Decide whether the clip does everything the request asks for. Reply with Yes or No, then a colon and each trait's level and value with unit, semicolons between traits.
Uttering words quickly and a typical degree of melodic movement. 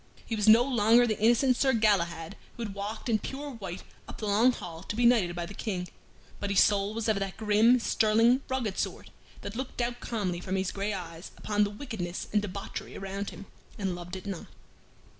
Yes: fast, 210 wpm; average, 3.2 semitones